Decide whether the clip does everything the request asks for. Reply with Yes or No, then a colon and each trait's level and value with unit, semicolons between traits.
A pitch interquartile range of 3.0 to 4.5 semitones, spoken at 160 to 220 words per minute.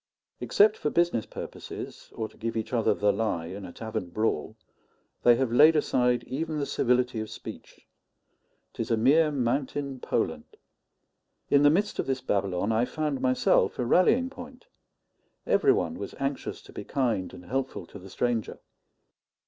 No: average, 5.1 semitones; average, 165 wpm